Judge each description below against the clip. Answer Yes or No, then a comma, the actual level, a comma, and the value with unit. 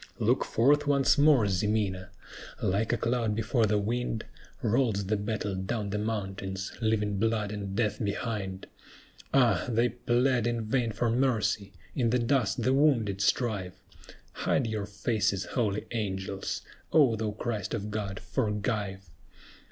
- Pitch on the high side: No, low, 110 Hz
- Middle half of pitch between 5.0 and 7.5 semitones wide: No, average, 3.0 semitones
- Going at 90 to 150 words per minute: Yes, average, 140 wpm